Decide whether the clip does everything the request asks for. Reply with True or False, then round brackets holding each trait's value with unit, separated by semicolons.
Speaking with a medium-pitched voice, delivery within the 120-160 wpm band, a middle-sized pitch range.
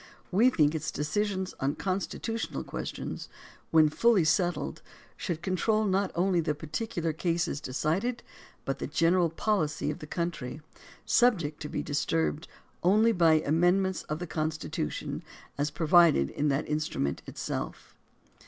True (165 Hz; 140 wpm; 3.8 semitones)